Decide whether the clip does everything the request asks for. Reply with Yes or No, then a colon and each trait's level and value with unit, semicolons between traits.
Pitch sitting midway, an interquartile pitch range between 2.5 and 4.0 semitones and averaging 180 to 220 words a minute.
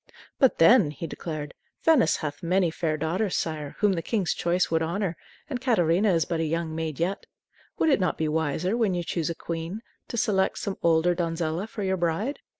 Yes: medium, 170 Hz; average, 3.6 semitones; average, 200 wpm